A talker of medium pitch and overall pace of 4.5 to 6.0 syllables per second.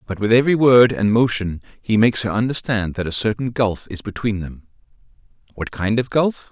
No: low, 110 Hz; 5.4 syllables/s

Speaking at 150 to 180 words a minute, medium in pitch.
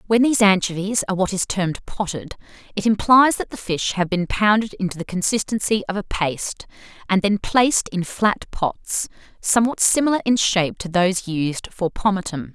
No: average, 175 wpm; high, 195 Hz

